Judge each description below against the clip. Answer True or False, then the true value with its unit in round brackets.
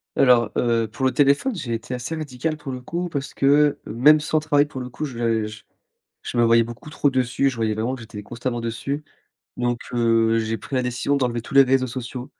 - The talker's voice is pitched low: True (125 Hz)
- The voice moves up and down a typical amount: True (3.2 semitones)